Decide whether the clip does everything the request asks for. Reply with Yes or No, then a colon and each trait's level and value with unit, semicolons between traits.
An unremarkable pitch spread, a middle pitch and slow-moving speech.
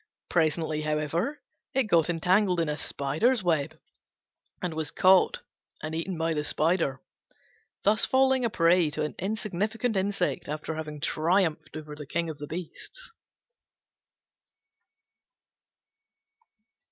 Yes: average, 4.3 semitones; medium, 165 Hz; slow, 120 wpm